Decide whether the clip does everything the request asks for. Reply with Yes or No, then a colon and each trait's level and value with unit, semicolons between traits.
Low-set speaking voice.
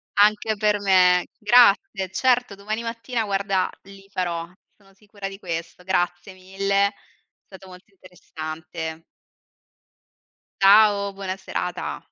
No: high, 195 Hz